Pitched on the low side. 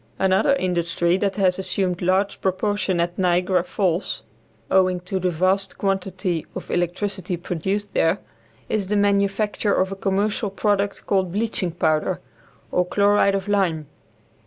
No: high, 190 Hz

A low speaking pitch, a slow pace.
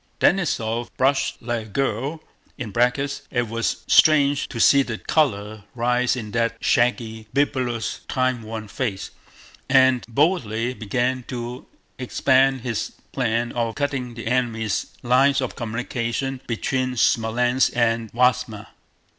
Yes: low, 120 Hz; slow, 120 wpm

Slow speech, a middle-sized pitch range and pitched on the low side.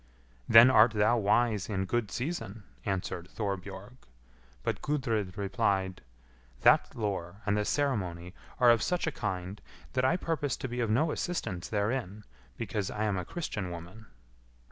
No: average, 150 wpm; average, 4.1 semitones; low, 105 Hz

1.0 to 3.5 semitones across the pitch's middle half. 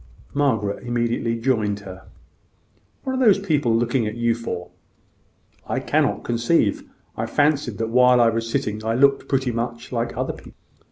Yes: average, 2.8 semitones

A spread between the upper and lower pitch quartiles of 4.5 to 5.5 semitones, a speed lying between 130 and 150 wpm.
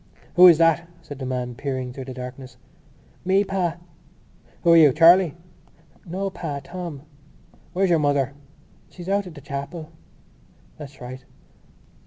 Yes: average, 4.8 semitones; average, 145 wpm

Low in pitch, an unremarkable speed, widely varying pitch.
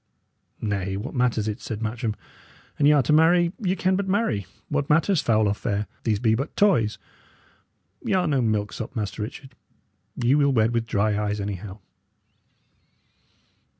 Yes: low, 115 Hz; average, 160 wpm; wide, 6.0 semitones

